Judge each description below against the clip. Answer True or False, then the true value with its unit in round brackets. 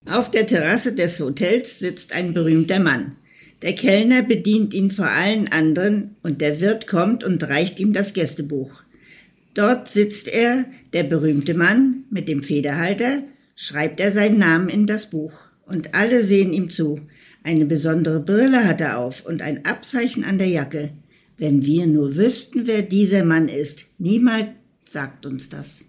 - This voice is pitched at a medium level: True (180 Hz)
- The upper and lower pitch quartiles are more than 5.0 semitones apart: True (5.4 semitones)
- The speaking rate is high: False (160 wpm)